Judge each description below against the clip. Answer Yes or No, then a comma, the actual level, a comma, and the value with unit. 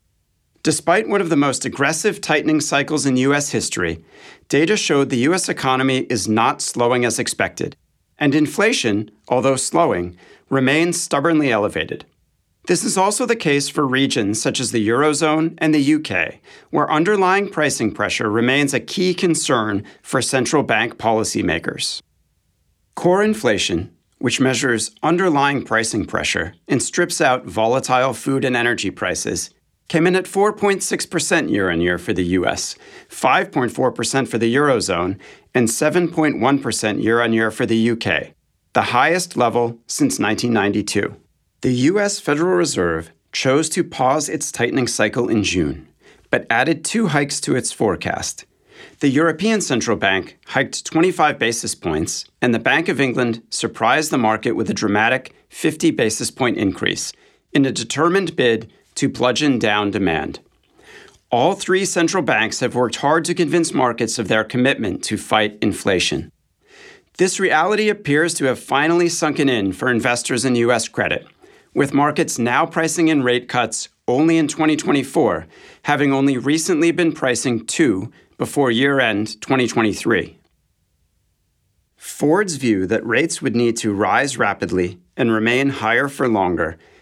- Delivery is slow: No, average, 145 wpm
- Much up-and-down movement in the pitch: Yes, wide, 6.0 semitones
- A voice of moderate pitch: No, low, 130 Hz